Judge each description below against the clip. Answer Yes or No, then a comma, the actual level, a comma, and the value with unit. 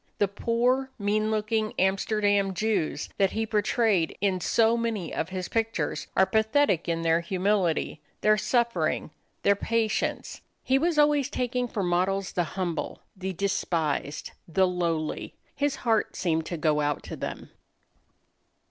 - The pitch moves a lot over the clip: No, average, 4.3 semitones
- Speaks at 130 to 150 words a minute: Yes, average, 140 wpm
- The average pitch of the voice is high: Yes, high, 200 Hz